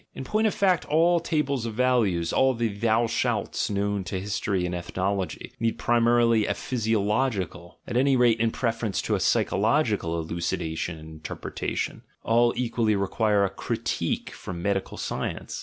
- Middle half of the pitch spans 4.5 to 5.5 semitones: No, average, 4.0 semitones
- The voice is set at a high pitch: No, low, 110 Hz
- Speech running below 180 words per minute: Yes, average, 155 wpm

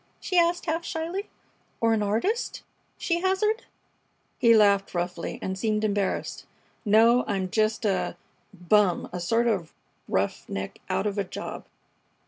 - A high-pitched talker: Yes, high, 215 Hz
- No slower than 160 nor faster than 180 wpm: No, slow, 135 wpm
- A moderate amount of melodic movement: No, wide, 8.7 semitones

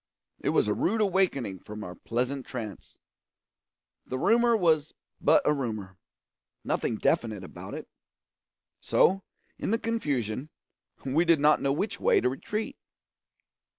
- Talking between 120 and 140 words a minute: Yes, slow, 135 wpm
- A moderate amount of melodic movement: No, wide, 9.0 semitones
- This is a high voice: No, medium, 140 Hz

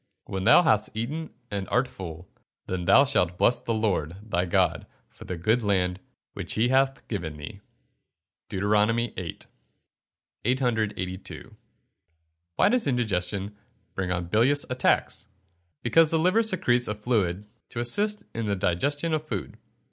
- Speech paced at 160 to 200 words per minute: No, average, 145 wpm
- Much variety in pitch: Yes, wide, 5.8 semitones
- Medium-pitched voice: No, low, 110 Hz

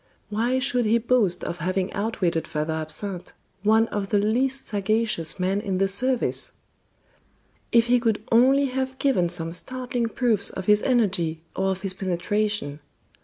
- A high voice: Yes, high, 210 Hz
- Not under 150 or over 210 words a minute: Yes, average, 155 wpm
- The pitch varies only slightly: No, average, 4.4 semitones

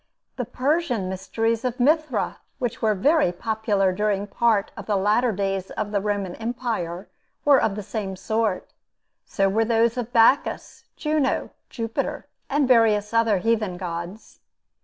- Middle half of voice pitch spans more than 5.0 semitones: No, average, 3.5 semitones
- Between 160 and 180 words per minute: No, average, 145 wpm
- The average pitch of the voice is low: No, high, 220 Hz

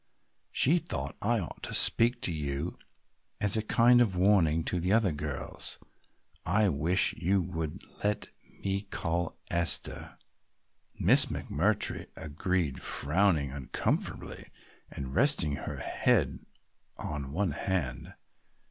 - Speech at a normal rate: No, slow, 120 wpm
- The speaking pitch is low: Yes, very low, 90 Hz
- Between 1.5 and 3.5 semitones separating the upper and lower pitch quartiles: No, average, 5.2 semitones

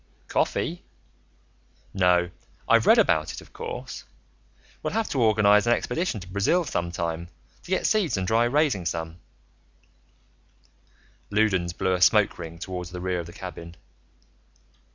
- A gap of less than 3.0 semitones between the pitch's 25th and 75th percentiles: No, average, 5.2 semitones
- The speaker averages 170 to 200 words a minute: No, average, 140 wpm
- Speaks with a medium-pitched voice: No, very low, 95 Hz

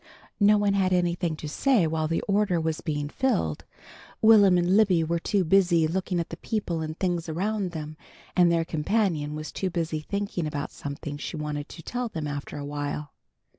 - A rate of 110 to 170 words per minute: No, average, 185 wpm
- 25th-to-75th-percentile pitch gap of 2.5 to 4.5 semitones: Yes, average, 4.0 semitones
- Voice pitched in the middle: Yes, medium, 170 Hz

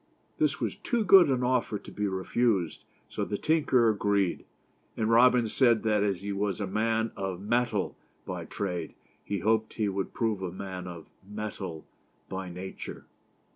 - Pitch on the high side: No, low, 105 Hz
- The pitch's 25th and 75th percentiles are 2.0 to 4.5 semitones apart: Yes, average, 3.2 semitones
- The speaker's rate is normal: Yes, average, 165 wpm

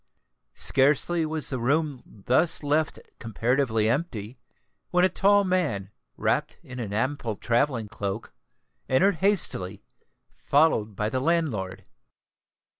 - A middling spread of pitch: No, wide, 6.4 semitones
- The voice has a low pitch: Yes, low, 130 Hz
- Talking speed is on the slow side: Yes, slow, 115 wpm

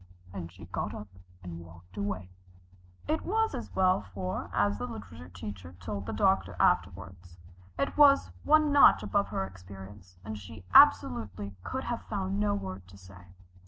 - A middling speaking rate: Yes, average, 160 wpm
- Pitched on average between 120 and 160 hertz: No, very low, 95 Hz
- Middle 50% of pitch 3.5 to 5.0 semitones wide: No, narrow, 2.4 semitones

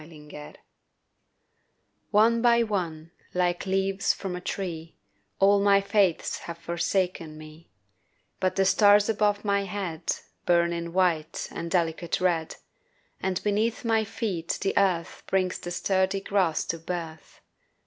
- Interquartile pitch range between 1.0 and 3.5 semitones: Yes, average, 3.1 semitones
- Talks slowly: Yes, slow, 130 wpm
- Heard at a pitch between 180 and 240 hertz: Yes, medium, 185 Hz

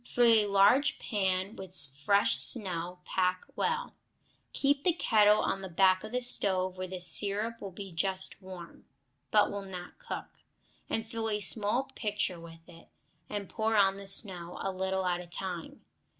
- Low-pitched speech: No, high, 195 Hz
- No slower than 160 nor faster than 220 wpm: Yes, average, 170 wpm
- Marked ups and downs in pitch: No, average, 2.8 semitones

